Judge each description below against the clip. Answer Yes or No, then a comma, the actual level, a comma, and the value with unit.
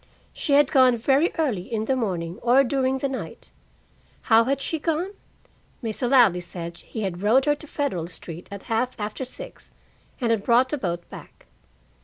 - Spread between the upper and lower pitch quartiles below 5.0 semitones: No, wide, 5.4 semitones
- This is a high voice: Yes, high, 240 Hz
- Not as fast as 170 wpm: No, average, 180 wpm